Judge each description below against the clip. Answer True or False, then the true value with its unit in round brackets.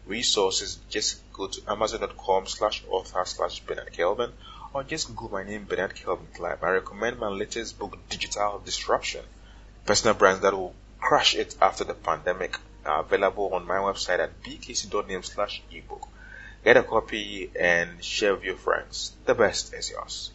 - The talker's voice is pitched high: True (380 Hz)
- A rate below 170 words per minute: True (160 wpm)